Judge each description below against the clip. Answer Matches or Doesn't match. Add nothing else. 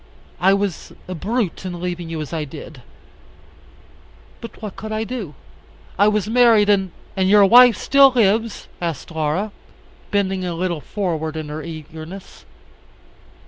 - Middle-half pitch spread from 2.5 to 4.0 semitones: Doesn't match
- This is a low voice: Doesn't match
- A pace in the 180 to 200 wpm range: Doesn't match